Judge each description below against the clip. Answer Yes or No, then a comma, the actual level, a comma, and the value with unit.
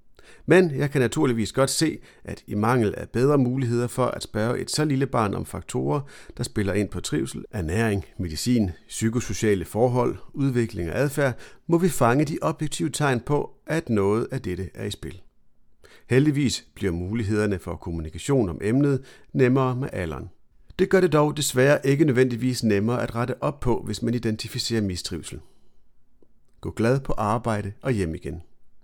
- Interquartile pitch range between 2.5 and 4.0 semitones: No, average, 4.8 semitones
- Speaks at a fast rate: No, average, 165 wpm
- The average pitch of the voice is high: No, low, 120 Hz